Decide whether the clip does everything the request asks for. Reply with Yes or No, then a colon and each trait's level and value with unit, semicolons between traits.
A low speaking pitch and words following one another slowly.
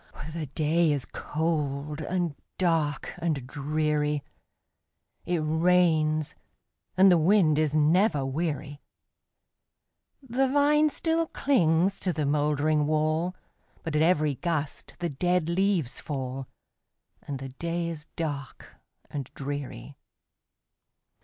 No: medium, 155 Hz; slow, 110 wpm